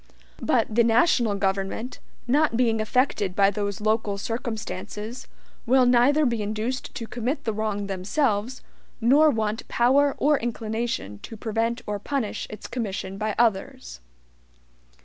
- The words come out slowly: Yes, slow, 130 wpm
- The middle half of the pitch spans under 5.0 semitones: Yes, average, 3.2 semitones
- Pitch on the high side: Yes, high, 225 Hz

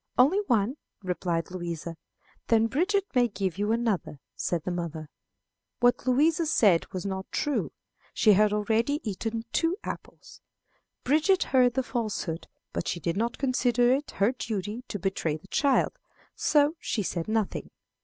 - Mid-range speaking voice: No, high, 225 Hz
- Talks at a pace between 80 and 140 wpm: No, average, 150 wpm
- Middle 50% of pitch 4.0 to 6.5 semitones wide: Yes, wide, 5.5 semitones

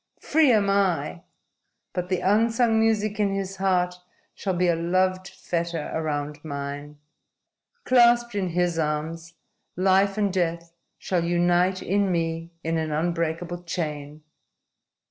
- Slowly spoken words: Yes, slow, 125 wpm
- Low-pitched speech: No, medium, 175 Hz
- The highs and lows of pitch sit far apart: No, average, 3.1 semitones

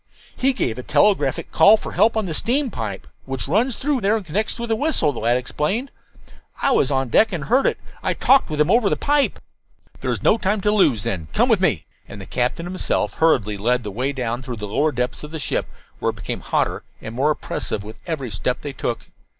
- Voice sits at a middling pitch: Yes, medium, 150 Hz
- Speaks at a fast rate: Yes, fast, 230 wpm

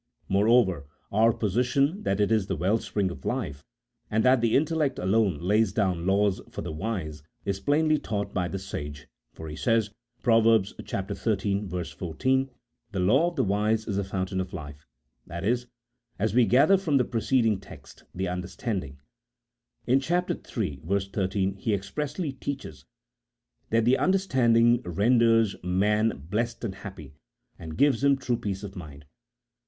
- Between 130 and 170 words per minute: Yes, average, 165 wpm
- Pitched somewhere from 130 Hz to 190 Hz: No, low, 105 Hz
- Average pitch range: Yes, average, 4.5 semitones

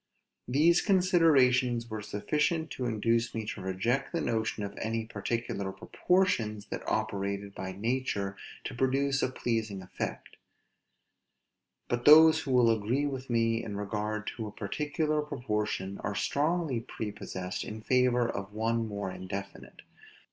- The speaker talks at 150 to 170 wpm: No, slow, 135 wpm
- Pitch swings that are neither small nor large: Yes, average, 4.6 semitones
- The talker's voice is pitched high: No, low, 115 Hz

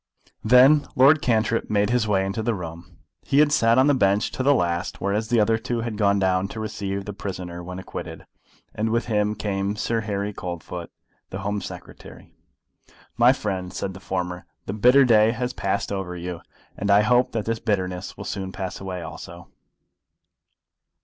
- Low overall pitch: Yes, low, 105 Hz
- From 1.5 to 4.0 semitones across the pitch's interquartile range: Yes, average, 3.3 semitones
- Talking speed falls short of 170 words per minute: No, average, 185 wpm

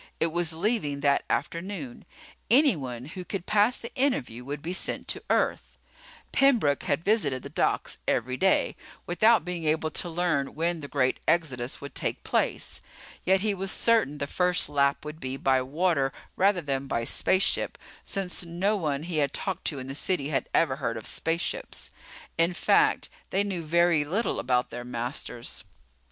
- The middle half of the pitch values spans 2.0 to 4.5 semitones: No, average, 5.2 semitones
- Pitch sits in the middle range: Yes, medium, 160 Hz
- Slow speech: No, average, 170 wpm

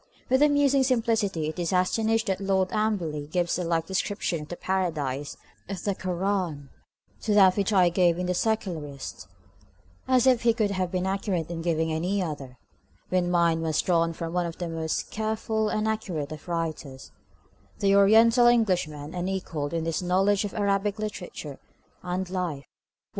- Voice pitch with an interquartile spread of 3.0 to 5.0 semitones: Yes, average, 3.8 semitones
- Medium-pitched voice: Yes, medium, 180 Hz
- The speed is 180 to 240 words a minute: No, average, 170 wpm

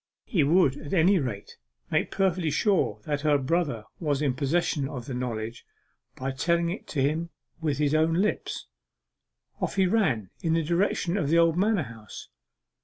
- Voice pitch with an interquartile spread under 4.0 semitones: No, average, 4.5 semitones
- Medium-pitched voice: Yes, medium, 155 Hz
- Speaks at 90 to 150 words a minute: No, average, 170 wpm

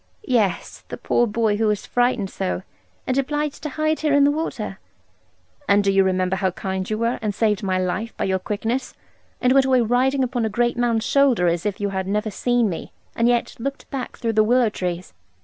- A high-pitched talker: Yes, high, 225 Hz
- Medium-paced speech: No, fast, 215 wpm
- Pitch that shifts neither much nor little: Yes, average, 4.5 semitones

